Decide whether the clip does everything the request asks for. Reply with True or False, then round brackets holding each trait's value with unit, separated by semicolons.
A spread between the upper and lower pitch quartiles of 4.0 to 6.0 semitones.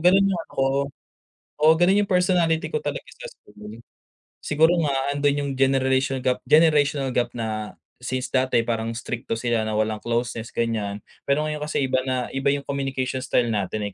True (4.3 semitones)